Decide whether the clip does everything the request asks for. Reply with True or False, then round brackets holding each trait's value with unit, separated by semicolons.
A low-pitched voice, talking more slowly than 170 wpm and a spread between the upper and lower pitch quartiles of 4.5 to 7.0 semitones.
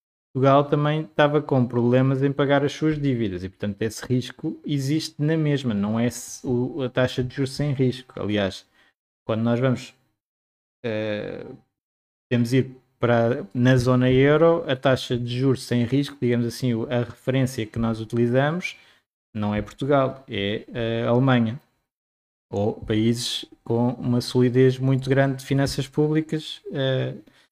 False (125 Hz; 145 wpm; 3.0 semitones)